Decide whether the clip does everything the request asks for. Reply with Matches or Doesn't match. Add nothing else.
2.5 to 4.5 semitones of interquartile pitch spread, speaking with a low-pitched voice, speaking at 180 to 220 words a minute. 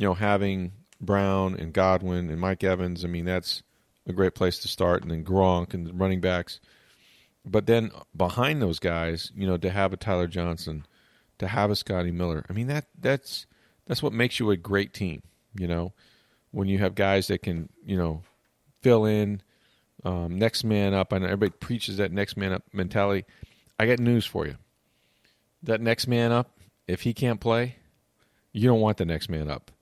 Matches